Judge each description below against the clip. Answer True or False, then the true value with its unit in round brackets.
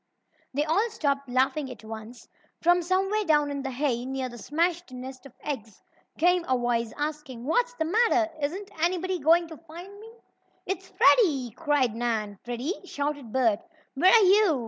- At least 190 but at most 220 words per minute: False (170 wpm)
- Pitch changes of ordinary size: False (5.9 semitones)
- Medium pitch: False (295 Hz)